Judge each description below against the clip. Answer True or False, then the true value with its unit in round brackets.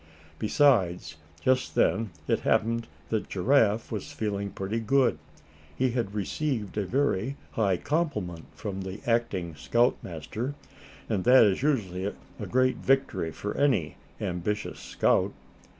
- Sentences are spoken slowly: True (125 wpm)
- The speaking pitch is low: True (110 Hz)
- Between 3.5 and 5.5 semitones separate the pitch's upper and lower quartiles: True (5.2 semitones)